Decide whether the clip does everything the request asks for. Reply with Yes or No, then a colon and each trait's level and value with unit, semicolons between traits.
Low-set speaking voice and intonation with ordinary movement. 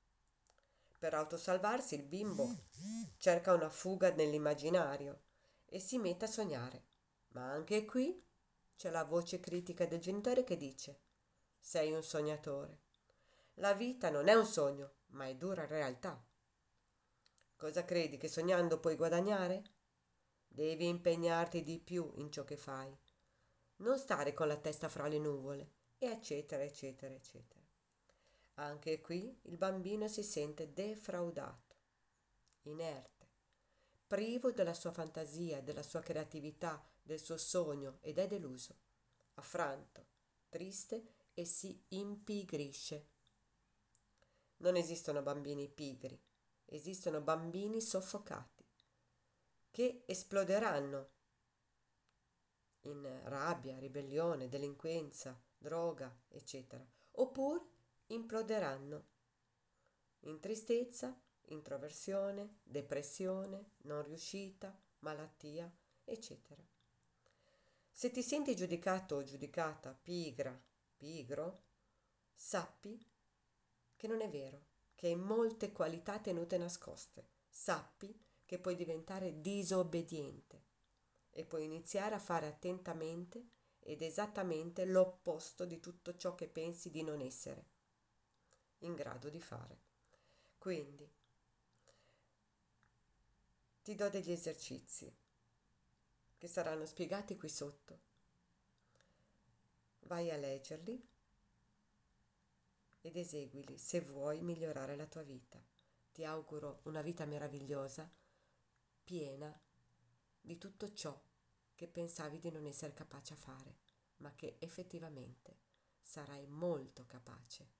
No: medium, 160 Hz; average, 4.5 semitones